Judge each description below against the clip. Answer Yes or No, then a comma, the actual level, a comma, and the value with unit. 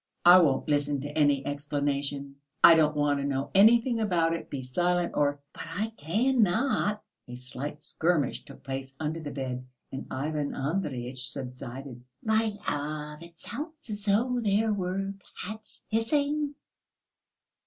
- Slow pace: No, average, 145 wpm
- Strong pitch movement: Yes, wide, 6.8 semitones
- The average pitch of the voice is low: No, medium, 155 Hz